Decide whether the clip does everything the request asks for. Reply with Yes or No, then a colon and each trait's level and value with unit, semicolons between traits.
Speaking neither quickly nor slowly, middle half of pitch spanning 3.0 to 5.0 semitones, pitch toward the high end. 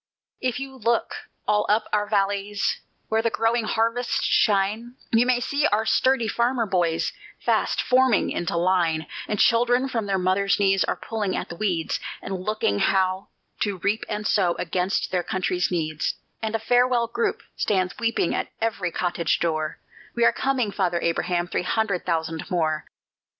Yes: average, 165 wpm; average, 4.3 semitones; high, 205 Hz